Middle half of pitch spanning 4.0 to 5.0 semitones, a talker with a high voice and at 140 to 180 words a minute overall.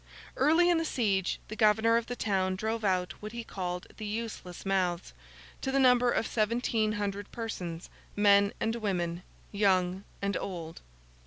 No: average, 3.5 semitones; high, 205 Hz; average, 160 wpm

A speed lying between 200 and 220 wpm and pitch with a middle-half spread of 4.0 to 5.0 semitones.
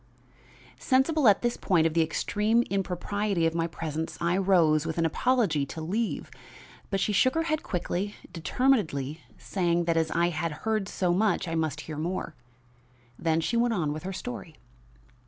No: average, 175 wpm; average, 4.7 semitones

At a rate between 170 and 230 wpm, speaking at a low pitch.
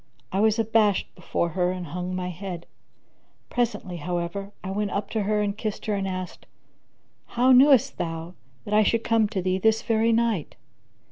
No: average, 180 wpm; high, 200 Hz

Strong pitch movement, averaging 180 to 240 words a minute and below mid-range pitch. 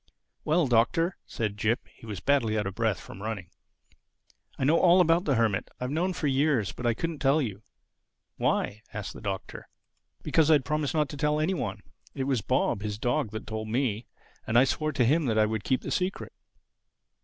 Yes: wide, 5.9 semitones; average, 200 wpm; low, 125 Hz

